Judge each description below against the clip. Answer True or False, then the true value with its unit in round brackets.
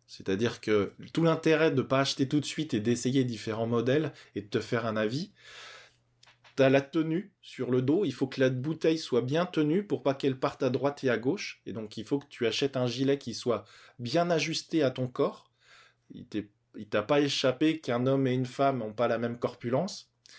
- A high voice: False (135 Hz)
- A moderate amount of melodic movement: True (3.6 semitones)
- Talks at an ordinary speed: False (225 wpm)